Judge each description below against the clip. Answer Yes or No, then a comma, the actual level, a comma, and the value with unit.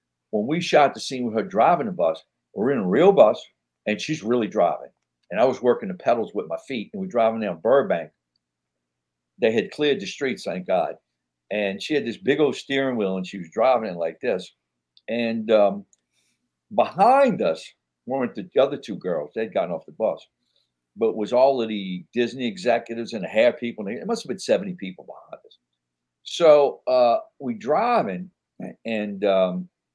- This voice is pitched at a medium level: No, low, 110 Hz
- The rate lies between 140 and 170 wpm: No, average, 190 wpm